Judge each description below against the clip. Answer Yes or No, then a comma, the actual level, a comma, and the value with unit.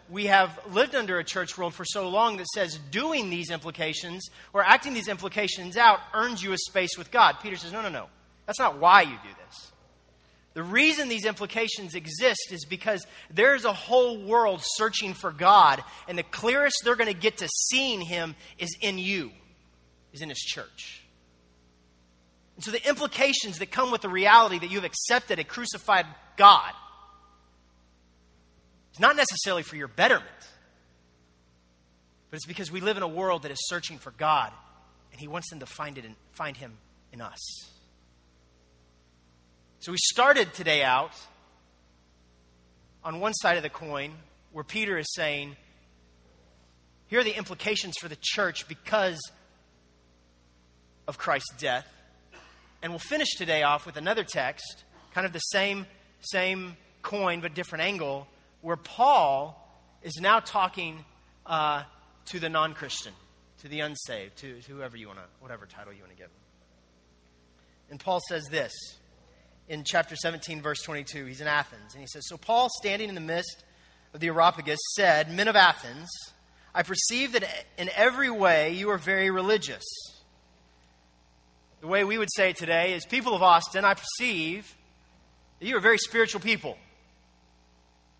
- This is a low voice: No, medium, 160 Hz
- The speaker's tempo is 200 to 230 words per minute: No, average, 160 wpm